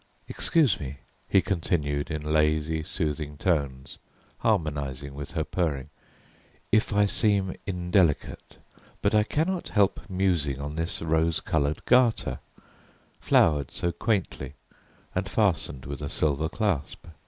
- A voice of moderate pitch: No, very low, 80 Hz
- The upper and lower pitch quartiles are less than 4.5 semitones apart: No, average, 5.0 semitones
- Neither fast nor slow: No, slow, 120 wpm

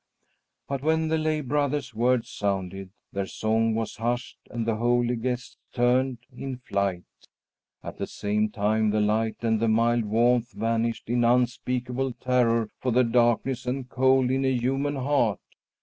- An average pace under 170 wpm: Yes, average, 155 wpm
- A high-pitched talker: No, low, 120 Hz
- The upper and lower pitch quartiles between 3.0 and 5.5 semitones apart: No, narrow, 2.5 semitones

